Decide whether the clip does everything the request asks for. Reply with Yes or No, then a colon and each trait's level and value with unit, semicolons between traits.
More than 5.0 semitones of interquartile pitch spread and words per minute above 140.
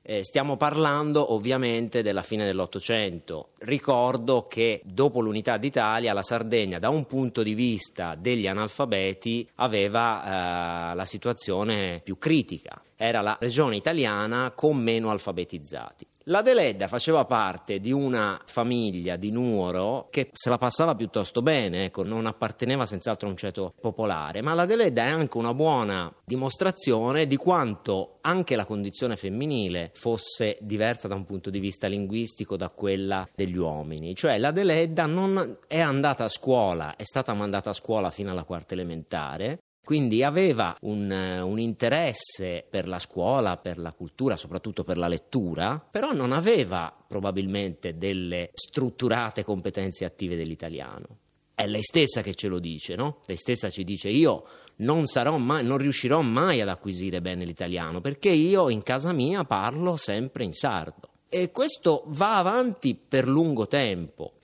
Yes: wide, 5.5 semitones; average, 150 wpm